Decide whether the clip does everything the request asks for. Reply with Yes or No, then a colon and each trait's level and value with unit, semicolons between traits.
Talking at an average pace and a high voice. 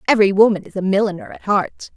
No: fast, 215 wpm; high, 200 Hz